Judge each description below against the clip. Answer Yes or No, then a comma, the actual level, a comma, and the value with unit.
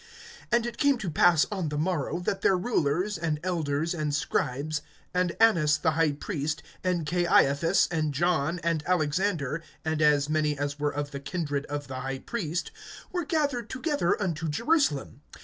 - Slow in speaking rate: No, average, 165 wpm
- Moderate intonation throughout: Yes, average, 3.8 semitones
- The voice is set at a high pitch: No, medium, 160 Hz